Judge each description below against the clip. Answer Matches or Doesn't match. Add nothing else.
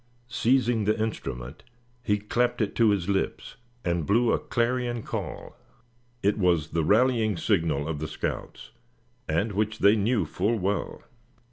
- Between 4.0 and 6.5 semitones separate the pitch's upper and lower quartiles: Matches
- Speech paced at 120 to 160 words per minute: Matches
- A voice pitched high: Doesn't match